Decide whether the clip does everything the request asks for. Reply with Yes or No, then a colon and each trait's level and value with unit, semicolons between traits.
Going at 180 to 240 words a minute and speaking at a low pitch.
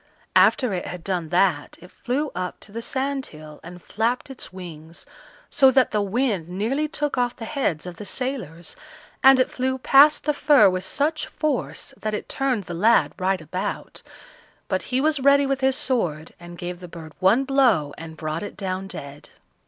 No: average, 185 wpm; high, 210 Hz